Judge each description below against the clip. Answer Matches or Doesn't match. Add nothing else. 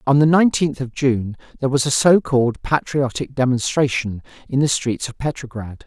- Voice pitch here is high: Doesn't match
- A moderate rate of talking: Matches